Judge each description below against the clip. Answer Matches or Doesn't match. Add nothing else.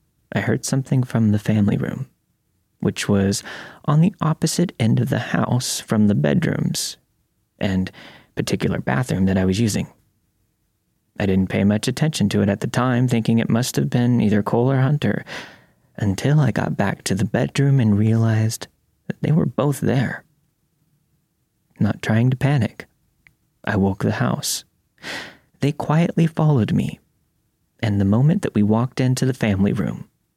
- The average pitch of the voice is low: Matches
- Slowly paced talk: Doesn't match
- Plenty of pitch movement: Matches